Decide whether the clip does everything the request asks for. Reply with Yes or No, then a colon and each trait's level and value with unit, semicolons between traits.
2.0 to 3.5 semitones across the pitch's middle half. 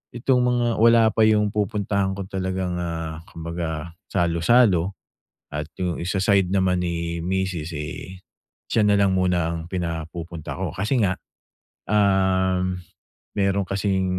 Yes: average, 2.9 semitones